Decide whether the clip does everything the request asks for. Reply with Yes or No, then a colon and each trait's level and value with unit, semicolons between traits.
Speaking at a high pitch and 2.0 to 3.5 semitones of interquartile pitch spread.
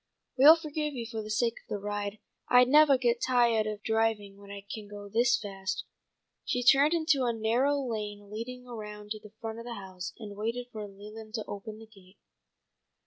Yes: high, 220 Hz; average, 3.1 semitones